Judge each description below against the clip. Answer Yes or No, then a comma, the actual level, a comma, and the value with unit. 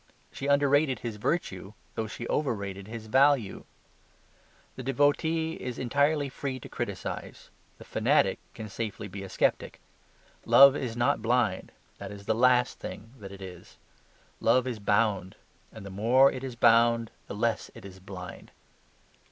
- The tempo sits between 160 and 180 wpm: No, average, 150 wpm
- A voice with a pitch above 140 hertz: No, low, 115 Hz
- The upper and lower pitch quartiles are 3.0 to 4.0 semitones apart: No, average, 4.6 semitones